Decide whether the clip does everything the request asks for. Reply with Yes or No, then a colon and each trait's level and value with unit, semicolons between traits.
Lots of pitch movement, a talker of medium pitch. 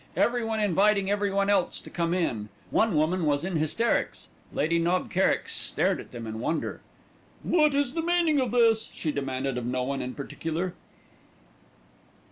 Yes: wide, 7.3 semitones; medium, 180 Hz